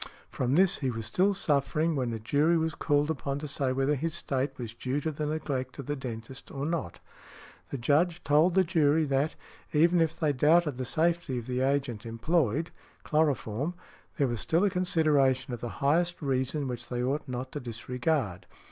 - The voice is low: No, medium, 145 Hz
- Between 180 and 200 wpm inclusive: Yes, average, 190 wpm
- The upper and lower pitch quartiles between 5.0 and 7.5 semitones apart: No, average, 3.8 semitones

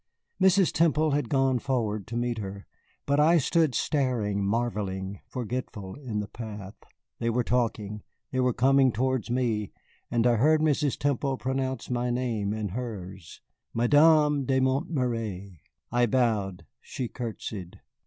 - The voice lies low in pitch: Yes, low, 120 Hz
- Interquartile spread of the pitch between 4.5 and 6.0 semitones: No, average, 4.1 semitones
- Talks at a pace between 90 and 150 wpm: Yes, average, 140 wpm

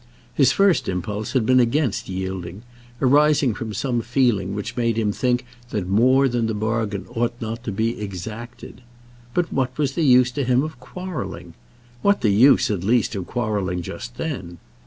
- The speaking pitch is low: Yes, low, 115 Hz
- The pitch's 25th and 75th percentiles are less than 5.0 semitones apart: Yes, average, 4.0 semitones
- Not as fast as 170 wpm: No, average, 175 wpm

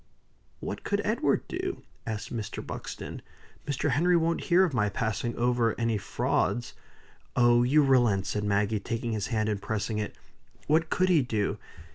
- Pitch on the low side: Yes, low, 115 Hz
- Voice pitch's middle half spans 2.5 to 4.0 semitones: No, average, 4.8 semitones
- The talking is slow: No, average, 160 wpm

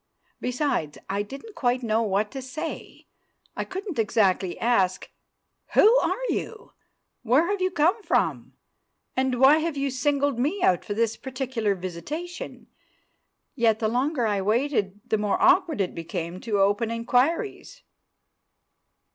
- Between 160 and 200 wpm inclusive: No, average, 140 wpm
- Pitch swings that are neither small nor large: No, wide, 6.3 semitones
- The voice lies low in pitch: No, high, 245 Hz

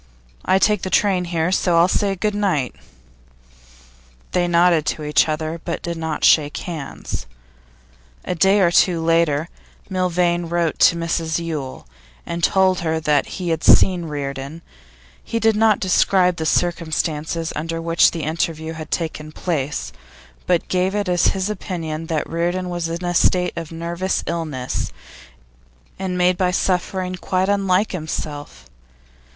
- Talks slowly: No, average, 150 wpm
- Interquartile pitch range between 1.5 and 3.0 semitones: Yes, narrow, 2.4 semitones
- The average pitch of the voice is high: No, medium, 170 Hz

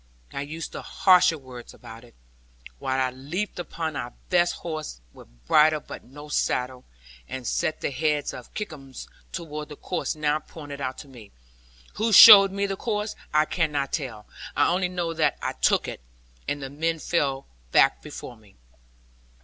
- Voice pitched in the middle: Yes, medium, 150 Hz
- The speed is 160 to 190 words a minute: Yes, average, 170 wpm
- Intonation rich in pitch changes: No, average, 4.4 semitones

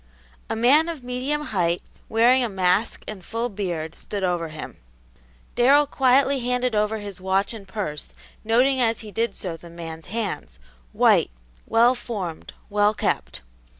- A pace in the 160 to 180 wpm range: No, average, 150 wpm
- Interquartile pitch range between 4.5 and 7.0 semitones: Yes, average, 5.2 semitones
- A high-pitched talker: Yes, high, 215 Hz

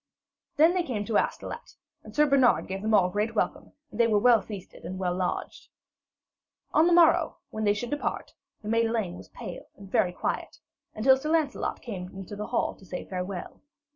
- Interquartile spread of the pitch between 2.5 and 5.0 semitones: No, wide, 5.6 semitones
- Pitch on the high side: Yes, high, 215 Hz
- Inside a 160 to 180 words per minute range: No, average, 200 wpm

